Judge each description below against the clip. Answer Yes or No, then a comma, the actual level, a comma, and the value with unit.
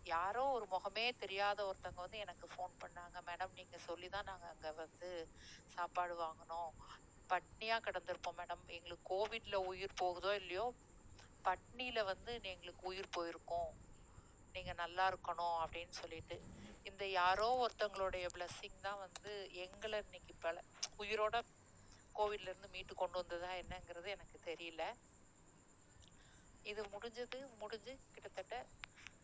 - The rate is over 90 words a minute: Yes, average, 115 wpm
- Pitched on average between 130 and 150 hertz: No, medium, 185 Hz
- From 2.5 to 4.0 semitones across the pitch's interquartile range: Yes, average, 2.8 semitones